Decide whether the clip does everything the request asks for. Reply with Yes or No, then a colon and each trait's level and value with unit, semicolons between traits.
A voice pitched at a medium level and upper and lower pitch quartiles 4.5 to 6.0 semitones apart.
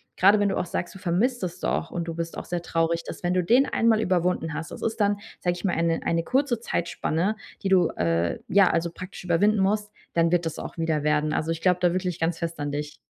No: medium, 175 Hz; average, 2.9 semitones